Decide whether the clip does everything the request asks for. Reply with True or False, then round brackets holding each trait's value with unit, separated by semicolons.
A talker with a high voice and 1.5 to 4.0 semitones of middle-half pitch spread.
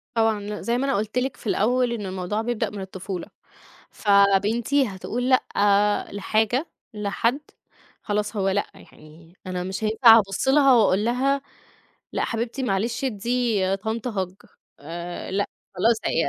True (210 Hz; 3.6 semitones)